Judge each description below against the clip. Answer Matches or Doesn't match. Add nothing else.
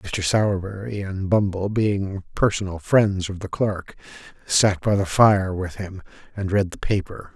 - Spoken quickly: Doesn't match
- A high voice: Doesn't match